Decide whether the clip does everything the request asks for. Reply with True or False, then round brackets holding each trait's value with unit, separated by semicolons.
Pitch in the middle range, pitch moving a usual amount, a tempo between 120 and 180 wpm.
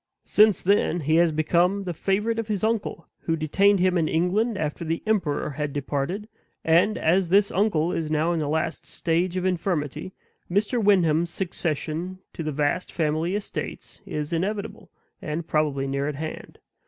True (170 Hz; 4.1 semitones; 165 wpm)